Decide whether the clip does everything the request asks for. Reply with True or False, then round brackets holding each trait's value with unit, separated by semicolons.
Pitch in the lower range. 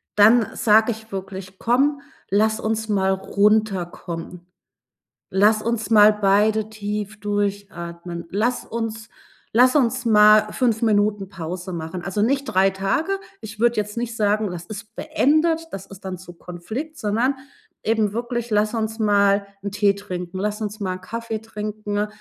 False (210 Hz)